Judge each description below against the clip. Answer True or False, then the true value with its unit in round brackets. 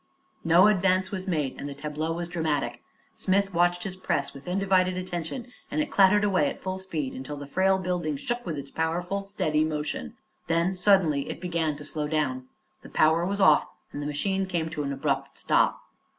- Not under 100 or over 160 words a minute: False (195 wpm)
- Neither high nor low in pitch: True (170 Hz)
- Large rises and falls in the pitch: False (4.1 semitones)